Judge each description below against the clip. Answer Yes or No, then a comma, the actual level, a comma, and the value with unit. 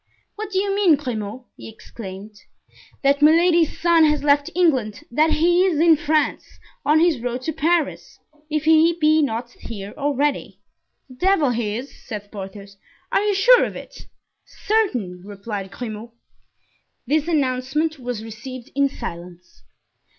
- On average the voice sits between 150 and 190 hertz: No, very high, 280 Hz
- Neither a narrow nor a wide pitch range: No, wide, 6.3 semitones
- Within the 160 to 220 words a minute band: No, average, 145 wpm